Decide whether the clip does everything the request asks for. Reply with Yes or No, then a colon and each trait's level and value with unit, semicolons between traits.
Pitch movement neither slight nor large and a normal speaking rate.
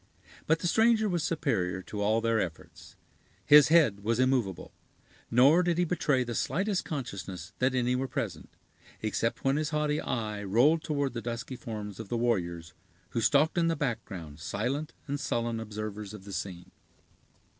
No: wide, 6.3 semitones; average, 165 wpm